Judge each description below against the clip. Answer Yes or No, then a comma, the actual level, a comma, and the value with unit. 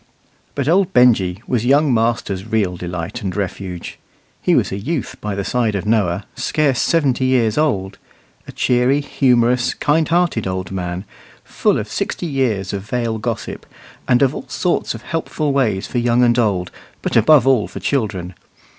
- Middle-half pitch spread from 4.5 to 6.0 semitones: Yes, wide, 5.4 semitones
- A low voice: Yes, low, 120 Hz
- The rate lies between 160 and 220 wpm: Yes, average, 170 wpm